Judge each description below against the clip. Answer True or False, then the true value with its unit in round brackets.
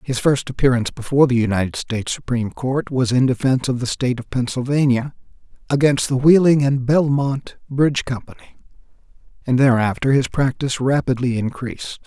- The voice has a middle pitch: False (130 Hz)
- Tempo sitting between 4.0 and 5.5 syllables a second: False (5.9 syllables/s)